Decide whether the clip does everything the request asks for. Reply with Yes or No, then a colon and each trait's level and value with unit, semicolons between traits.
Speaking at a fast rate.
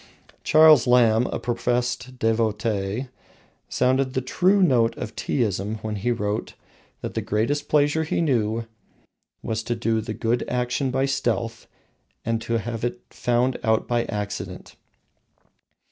No: slow, 135 wpm